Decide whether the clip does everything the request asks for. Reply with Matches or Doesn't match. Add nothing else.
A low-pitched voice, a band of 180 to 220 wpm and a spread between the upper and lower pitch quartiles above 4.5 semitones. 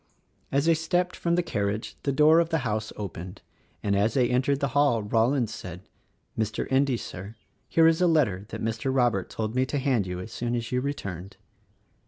Matches